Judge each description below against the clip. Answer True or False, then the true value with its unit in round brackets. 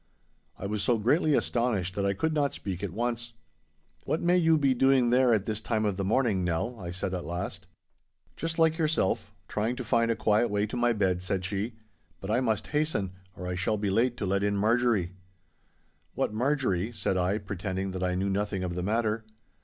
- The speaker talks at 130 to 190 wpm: False (205 wpm)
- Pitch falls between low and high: False (105 Hz)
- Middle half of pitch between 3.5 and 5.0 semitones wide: True (4.2 semitones)